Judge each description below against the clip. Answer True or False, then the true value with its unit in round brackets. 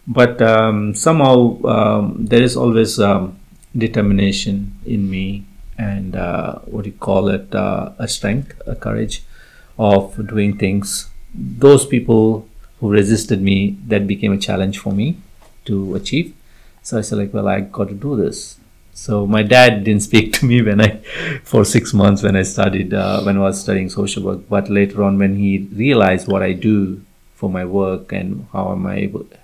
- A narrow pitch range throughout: True (2.1 semitones)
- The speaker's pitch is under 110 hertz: True (100 Hz)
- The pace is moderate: True (180 wpm)